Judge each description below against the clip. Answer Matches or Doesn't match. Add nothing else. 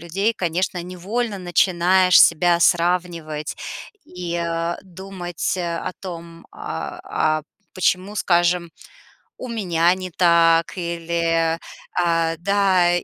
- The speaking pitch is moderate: Matches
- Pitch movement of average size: Doesn't match